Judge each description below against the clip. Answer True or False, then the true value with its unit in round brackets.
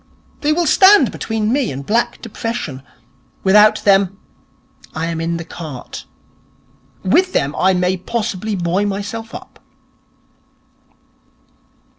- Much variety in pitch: False (4.8 semitones)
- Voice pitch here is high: True (200 Hz)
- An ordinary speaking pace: False (115 wpm)